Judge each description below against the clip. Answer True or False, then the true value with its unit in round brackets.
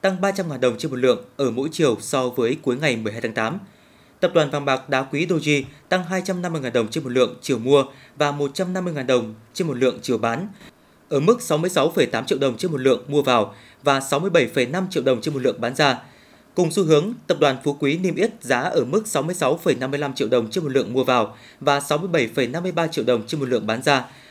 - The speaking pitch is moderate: True (145 Hz)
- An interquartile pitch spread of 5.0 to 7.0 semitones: True (5.5 semitones)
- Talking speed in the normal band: True (215 wpm)